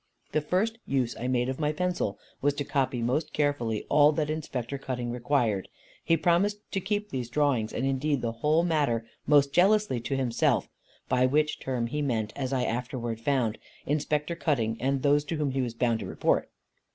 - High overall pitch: No, low, 135 Hz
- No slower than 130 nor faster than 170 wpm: No, average, 190 wpm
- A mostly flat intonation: No, average, 3.9 semitones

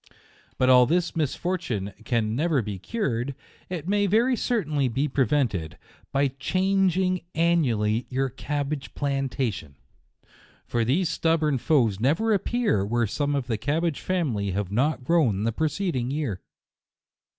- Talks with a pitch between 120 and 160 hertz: Yes, medium, 140 Hz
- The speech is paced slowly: Yes, slow, 130 wpm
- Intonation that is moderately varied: No, wide, 6.3 semitones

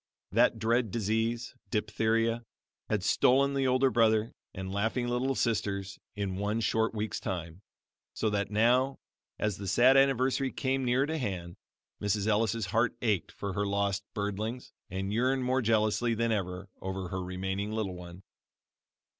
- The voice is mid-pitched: No, low, 110 Hz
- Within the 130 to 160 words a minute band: Yes, average, 150 wpm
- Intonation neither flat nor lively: Yes, average, 3.5 semitones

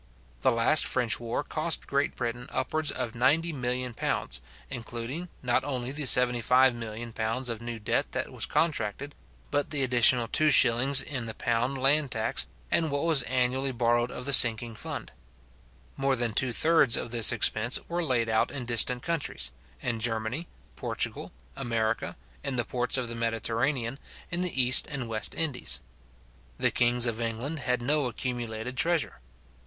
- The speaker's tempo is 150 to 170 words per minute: Yes, average, 155 wpm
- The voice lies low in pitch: Yes, low, 125 Hz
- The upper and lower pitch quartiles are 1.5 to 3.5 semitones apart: Yes, average, 2.9 semitones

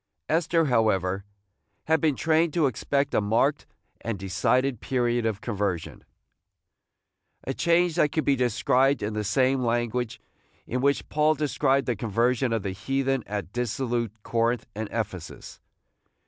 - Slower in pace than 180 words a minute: Yes, average, 145 wpm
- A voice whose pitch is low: Yes, low, 120 Hz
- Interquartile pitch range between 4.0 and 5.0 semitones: Yes, average, 4.3 semitones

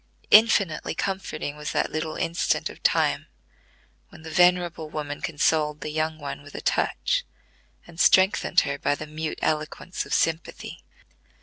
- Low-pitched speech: No, medium, 155 Hz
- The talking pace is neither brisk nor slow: Yes, average, 145 wpm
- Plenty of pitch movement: No, narrow, 2.5 semitones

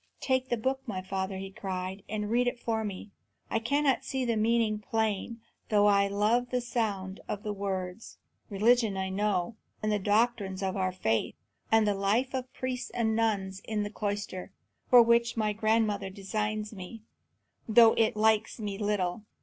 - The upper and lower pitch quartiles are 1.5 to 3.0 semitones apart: Yes, average, 2.7 semitones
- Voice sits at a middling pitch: No, high, 210 Hz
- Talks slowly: No, average, 175 wpm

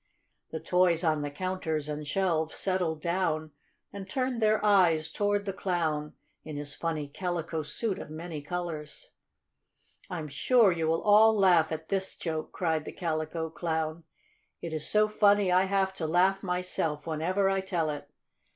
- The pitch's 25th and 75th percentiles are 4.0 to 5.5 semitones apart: No, average, 3.4 semitones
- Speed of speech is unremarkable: Yes, average, 160 wpm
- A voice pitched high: No, medium, 170 Hz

